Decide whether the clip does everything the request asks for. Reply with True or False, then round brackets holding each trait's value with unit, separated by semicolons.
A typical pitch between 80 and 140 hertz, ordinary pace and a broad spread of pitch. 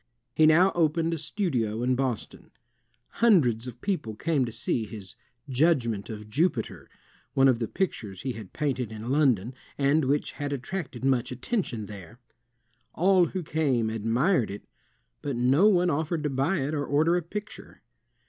True (135 Hz; 160 wpm; 5.9 semitones)